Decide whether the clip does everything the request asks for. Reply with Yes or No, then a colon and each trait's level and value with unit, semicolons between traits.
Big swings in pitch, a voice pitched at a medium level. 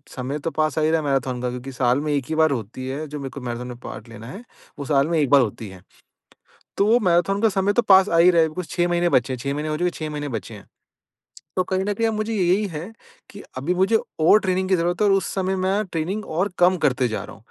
Yes: wide, 5.8 semitones; medium, 160 Hz